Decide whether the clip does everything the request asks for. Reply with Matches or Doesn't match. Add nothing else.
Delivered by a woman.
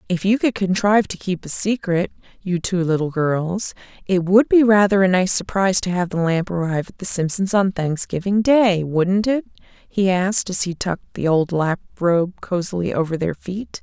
Matches